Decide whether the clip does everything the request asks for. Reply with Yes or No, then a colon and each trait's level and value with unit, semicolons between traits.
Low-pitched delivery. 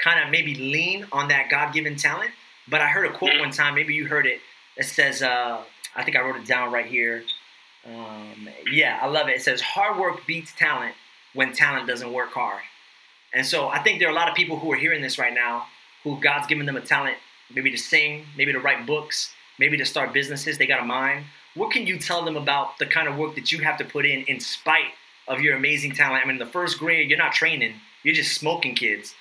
No: medium, 145 Hz